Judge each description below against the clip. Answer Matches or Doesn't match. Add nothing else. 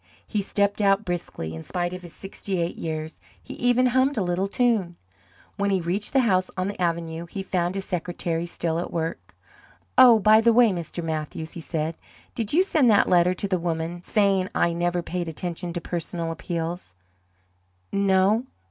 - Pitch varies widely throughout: Doesn't match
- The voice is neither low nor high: Matches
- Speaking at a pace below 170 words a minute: Doesn't match